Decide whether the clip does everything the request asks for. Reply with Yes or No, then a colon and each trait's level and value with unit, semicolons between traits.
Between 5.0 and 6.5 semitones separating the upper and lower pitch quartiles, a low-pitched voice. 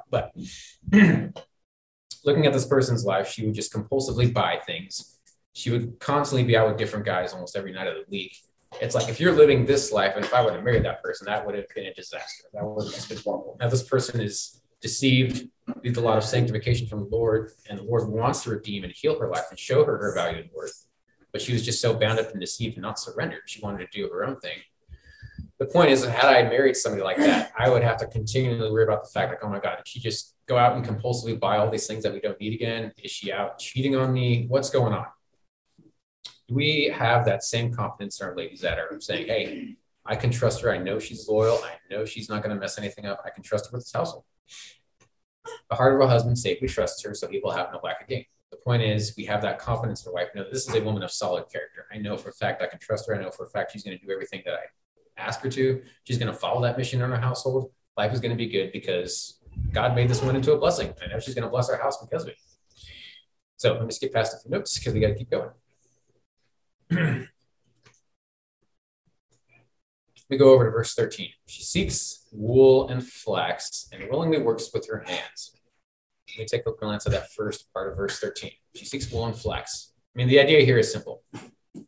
No: average, 3.6 semitones; low, 120 Hz